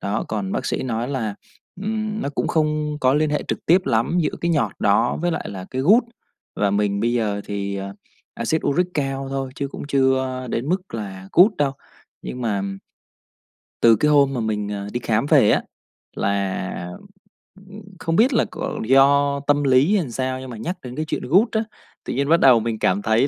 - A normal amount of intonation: No, wide, 5.7 semitones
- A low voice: Yes, low, 130 Hz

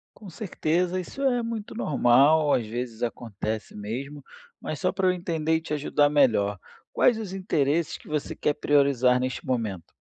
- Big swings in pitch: Yes, wide, 6.2 semitones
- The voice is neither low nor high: Yes, medium, 145 Hz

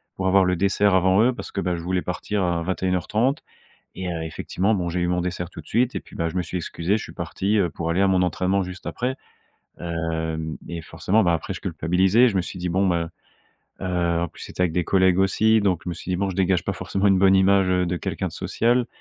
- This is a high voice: No, very low, 90 Hz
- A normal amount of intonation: No, narrow, 2.1 semitones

